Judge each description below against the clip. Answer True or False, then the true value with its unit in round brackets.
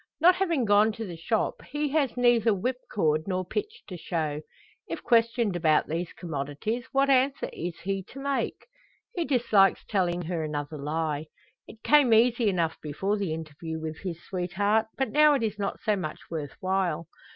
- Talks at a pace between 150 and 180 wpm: True (175 wpm)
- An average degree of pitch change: False (6.9 semitones)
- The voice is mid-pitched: False (195 Hz)